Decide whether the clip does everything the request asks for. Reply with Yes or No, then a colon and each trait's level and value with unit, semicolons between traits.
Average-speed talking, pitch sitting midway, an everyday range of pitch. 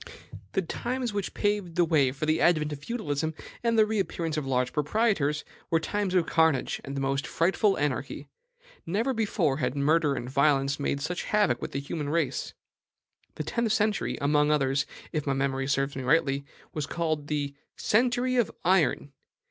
No: average, 170 wpm; medium, 155 Hz; wide, 5.8 semitones